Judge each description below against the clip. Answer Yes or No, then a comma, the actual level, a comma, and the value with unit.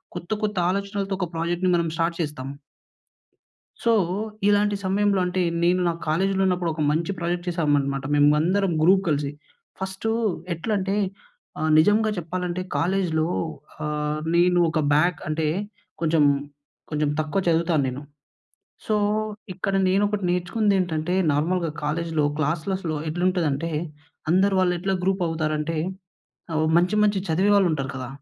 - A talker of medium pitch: Yes, medium, 175 Hz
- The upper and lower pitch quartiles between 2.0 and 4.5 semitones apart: Yes, average, 3.5 semitones